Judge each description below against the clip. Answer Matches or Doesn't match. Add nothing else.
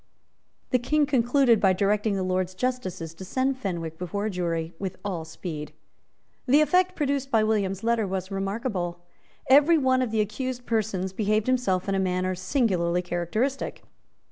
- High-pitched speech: Matches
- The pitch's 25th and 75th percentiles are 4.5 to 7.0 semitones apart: Matches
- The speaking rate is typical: Matches